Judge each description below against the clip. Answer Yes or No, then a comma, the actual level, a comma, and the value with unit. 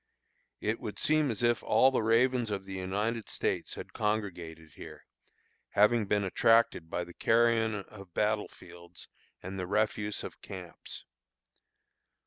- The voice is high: No, low, 105 Hz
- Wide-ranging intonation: No, average, 3.4 semitones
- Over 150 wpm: No, average, 140 wpm